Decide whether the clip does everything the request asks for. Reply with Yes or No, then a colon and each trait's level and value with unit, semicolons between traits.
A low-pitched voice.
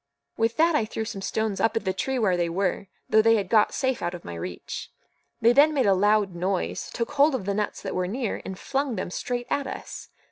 No: high, 215 Hz